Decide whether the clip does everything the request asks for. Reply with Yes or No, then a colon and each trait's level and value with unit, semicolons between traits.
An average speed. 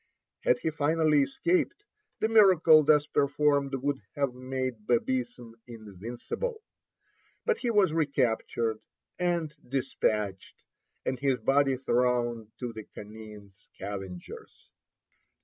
No: slow, 105 wpm